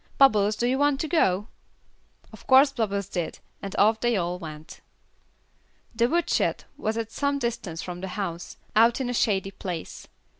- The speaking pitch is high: Yes, high, 215 Hz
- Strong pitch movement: No, average, 4.9 semitones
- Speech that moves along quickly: No, average, 165 wpm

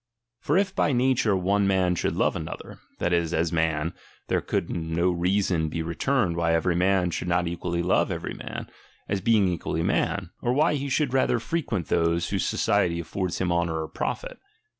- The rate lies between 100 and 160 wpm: No, average, 185 wpm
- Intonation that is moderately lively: Yes, average, 3.3 semitones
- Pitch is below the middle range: Yes, very low, 90 Hz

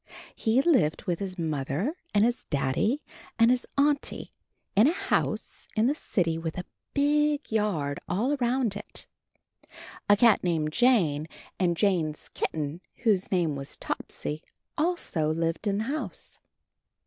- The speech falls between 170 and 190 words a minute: No, average, 140 wpm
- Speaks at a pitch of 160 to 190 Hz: No, high, 200 Hz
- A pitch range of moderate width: No, wide, 7.5 semitones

